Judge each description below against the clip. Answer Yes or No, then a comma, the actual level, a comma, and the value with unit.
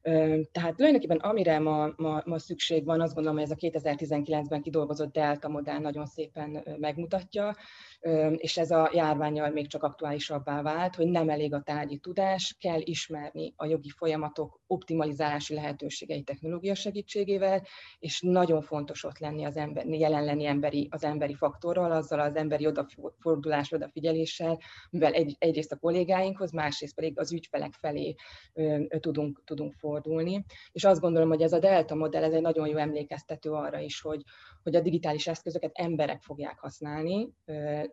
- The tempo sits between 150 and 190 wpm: Yes, fast, 155 wpm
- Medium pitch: Yes, medium, 155 Hz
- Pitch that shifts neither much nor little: No, narrow, 1.8 semitones